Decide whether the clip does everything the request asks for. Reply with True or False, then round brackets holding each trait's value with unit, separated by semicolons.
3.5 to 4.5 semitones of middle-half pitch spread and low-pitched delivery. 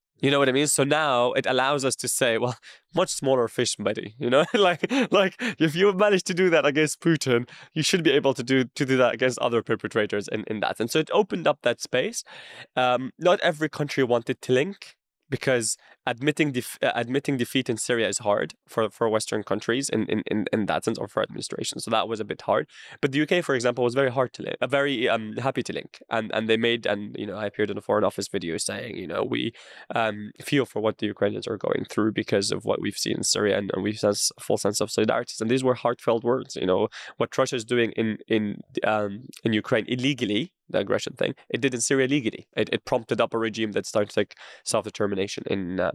True (4.2 semitones; 125 Hz)